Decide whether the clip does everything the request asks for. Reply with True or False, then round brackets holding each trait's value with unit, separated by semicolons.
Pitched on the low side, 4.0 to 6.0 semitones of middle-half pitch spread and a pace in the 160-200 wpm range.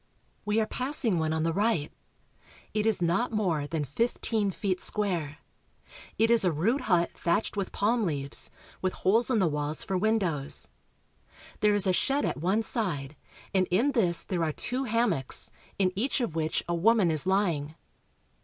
False (190 Hz; 5.3 semitones; 175 wpm)